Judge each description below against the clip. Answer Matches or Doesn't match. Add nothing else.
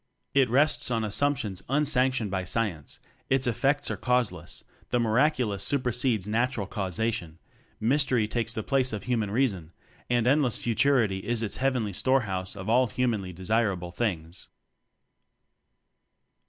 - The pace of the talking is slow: Matches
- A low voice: Matches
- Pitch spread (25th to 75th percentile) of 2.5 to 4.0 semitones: Doesn't match